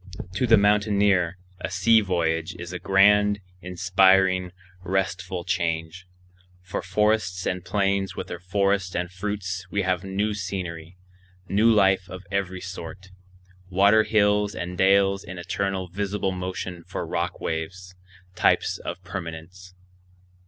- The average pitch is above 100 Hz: No, very low, 95 Hz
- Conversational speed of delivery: No, slow, 130 wpm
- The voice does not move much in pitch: Yes, narrow, 1.7 semitones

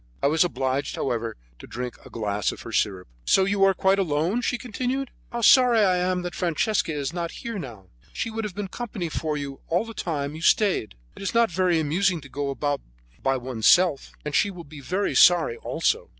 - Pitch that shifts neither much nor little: No, wide, 6.1 semitones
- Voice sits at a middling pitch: Yes, medium, 170 Hz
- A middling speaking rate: No, fast, 215 wpm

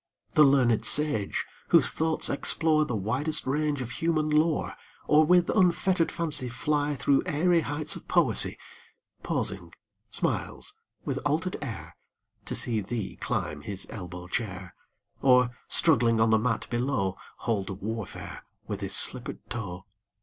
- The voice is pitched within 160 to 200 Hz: No, low, 130 Hz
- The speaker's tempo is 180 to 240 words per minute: No, slow, 135 wpm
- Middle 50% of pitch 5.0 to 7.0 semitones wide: Yes, wide, 5.6 semitones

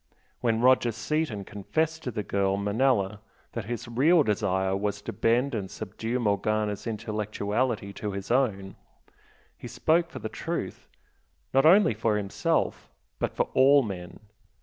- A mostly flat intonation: No, average, 4.2 semitones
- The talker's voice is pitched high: No, low, 110 Hz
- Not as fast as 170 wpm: Yes, average, 140 wpm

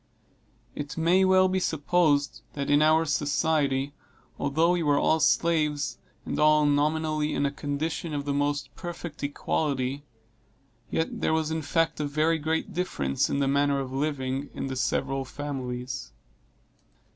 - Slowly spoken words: No, average, 150 wpm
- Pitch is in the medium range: Yes, medium, 145 Hz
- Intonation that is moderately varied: No, narrow, 2.2 semitones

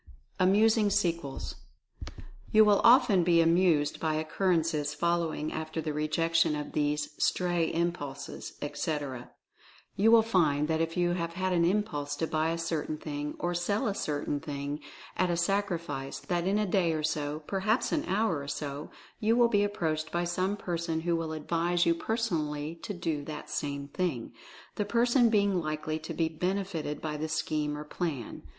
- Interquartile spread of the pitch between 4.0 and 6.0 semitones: No, average, 3.6 semitones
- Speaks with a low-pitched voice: No, medium, 165 Hz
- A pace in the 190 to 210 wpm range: No, average, 175 wpm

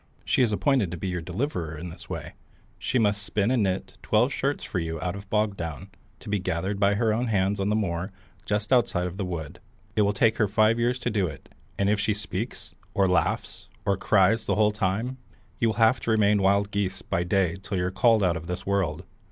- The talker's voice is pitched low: Yes, low, 100 Hz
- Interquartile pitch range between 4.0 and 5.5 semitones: No, average, 3.0 semitones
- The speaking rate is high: Yes, fast, 235 wpm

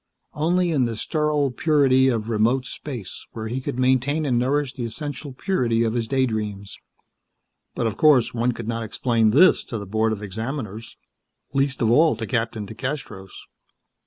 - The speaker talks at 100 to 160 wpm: No, average, 170 wpm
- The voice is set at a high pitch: No, low, 120 Hz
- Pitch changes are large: No, average, 3.8 semitones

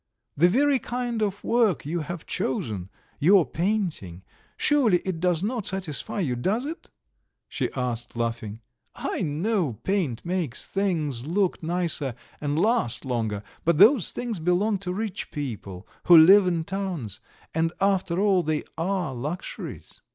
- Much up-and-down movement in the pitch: Yes, wide, 6.2 semitones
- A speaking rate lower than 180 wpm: Yes, average, 145 wpm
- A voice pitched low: No, medium, 175 Hz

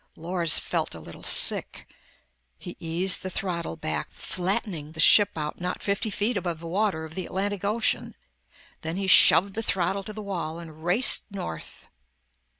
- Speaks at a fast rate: No, average, 165 wpm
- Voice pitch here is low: No, medium, 180 Hz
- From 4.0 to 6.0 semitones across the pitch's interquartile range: No, average, 3.3 semitones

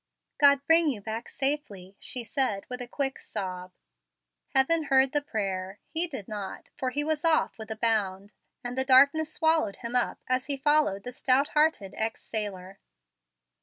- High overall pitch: Yes, very high, 255 Hz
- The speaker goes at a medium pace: Yes, average, 170 wpm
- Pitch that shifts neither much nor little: No, wide, 5.9 semitones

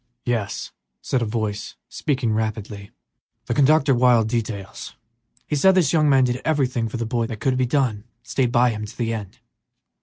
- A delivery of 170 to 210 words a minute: Yes, average, 190 wpm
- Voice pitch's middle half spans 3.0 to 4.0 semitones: Yes, average, 3.3 semitones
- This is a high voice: No, low, 120 Hz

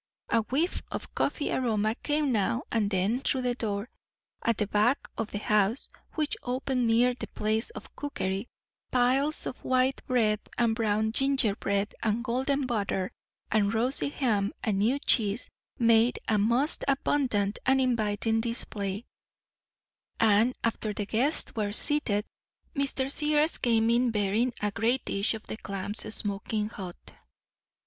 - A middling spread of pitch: Yes, average, 3.5 semitones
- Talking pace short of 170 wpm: Yes, average, 145 wpm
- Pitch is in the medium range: No, high, 225 Hz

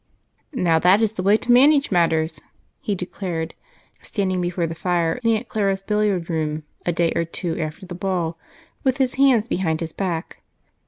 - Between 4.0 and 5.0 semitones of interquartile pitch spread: Yes, average, 4.3 semitones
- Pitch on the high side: No, medium, 180 Hz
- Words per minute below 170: No, average, 175 wpm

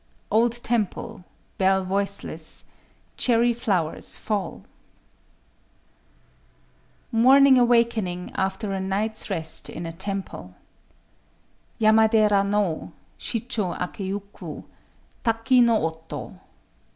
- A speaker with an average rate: No, slow, 80 wpm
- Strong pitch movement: No, average, 3.4 semitones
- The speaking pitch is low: No, high, 205 Hz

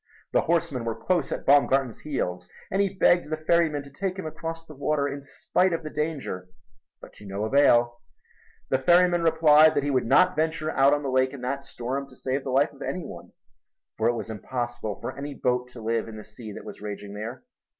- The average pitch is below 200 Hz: Yes, medium, 140 Hz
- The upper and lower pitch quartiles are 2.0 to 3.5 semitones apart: No, average, 4.7 semitones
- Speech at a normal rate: No, fast, 220 wpm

